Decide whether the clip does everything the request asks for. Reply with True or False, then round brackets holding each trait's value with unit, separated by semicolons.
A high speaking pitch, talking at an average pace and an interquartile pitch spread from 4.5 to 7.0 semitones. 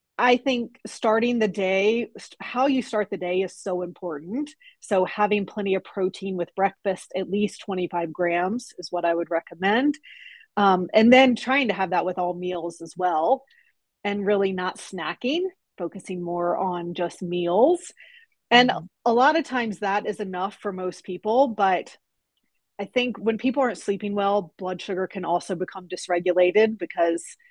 True (195 Hz; 165 wpm; 4.8 semitones)